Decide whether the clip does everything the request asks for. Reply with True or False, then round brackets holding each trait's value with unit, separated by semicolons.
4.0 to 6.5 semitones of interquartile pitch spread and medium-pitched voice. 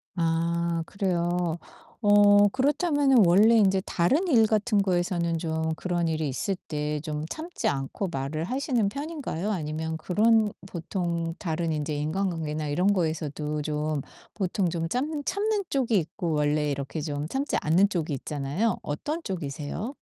True (5.3 semitones; 175 Hz)